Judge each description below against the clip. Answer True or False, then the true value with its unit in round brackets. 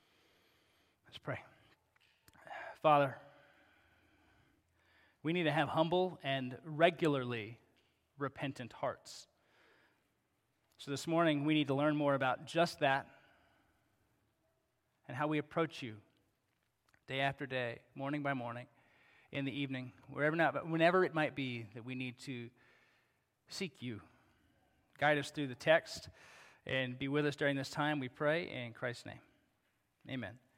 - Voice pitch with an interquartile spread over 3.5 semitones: False (3.2 semitones)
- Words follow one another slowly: True (130 wpm)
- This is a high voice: False (140 Hz)